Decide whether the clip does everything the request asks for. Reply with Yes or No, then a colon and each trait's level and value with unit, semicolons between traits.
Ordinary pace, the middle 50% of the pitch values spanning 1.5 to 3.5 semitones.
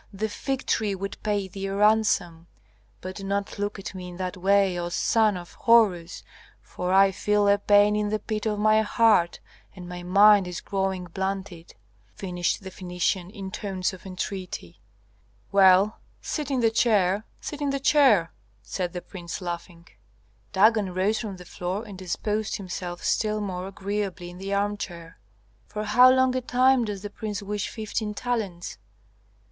Yes: average, 170 wpm; average, 2.7 semitones